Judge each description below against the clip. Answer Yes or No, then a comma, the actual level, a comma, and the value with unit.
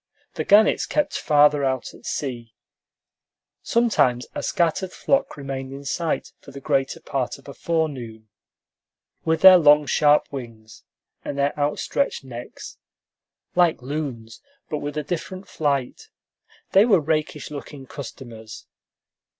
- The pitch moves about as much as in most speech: Yes, average, 3.4 semitones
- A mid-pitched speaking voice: Yes, medium, 145 Hz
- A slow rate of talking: Yes, slow, 130 wpm